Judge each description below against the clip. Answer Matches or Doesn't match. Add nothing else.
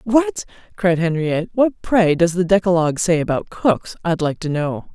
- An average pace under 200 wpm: Matches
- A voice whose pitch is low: Doesn't match